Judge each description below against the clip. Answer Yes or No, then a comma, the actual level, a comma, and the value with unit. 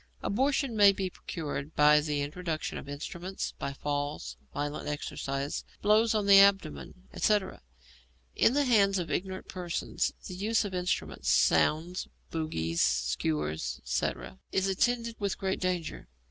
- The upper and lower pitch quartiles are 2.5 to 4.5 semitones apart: No, wide, 5.6 semitones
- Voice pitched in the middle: Yes, medium, 180 Hz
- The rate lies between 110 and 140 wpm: Yes, slow, 135 wpm